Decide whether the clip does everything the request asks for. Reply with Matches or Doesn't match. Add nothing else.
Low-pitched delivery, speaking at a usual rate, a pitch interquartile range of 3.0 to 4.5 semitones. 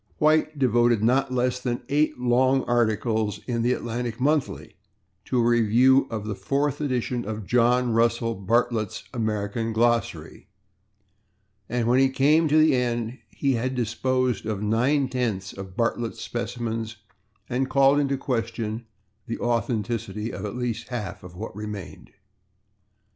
Doesn't match